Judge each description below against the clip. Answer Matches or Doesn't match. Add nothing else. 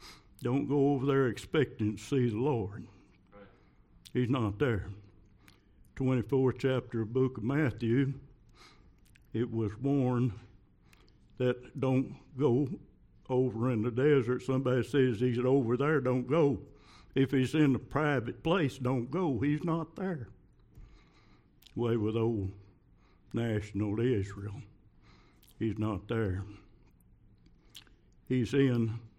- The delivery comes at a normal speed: Doesn't match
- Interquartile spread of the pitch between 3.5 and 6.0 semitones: Matches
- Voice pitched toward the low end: Matches